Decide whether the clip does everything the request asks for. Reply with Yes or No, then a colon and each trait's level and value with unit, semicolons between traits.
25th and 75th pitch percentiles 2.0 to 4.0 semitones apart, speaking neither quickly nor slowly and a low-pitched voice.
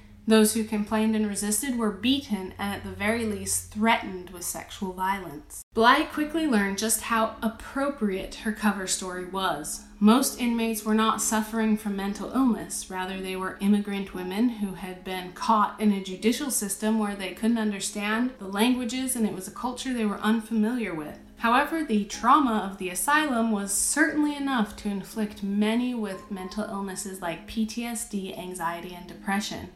No: average, 2.9 semitones; average, 165 wpm; high, 215 Hz